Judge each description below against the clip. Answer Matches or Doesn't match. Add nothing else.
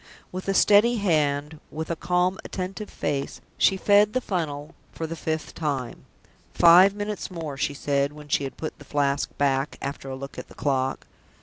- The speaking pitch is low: Doesn't match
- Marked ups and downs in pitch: Doesn't match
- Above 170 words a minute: Matches